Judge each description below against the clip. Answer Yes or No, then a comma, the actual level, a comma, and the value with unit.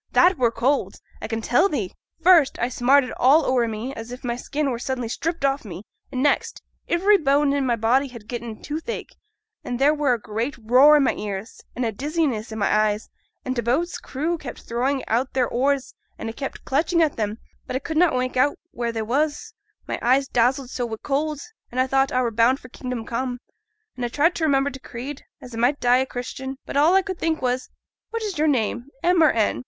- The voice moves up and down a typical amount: Yes, average, 3.5 semitones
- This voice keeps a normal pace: No, fast, 235 wpm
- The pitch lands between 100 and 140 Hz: No, very high, 260 Hz